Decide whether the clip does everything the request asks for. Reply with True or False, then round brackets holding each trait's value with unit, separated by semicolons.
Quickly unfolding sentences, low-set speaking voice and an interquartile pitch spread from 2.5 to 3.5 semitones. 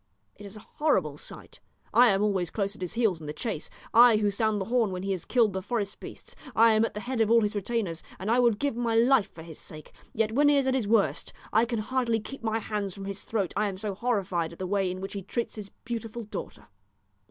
False (265 wpm; 215 Hz; 3.2 semitones)